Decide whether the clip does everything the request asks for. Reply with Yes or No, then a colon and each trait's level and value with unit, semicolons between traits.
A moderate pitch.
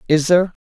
Yes: medium, 165 Hz